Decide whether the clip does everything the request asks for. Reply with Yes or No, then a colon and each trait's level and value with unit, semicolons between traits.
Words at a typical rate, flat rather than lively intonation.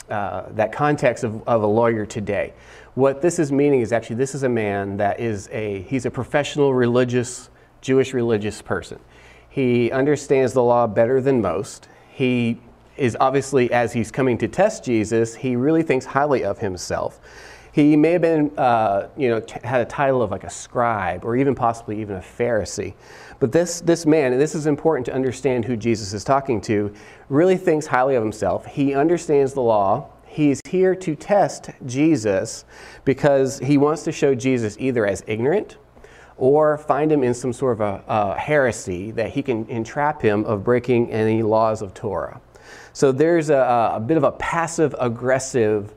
No: average, 180 wpm; average, 4.2 semitones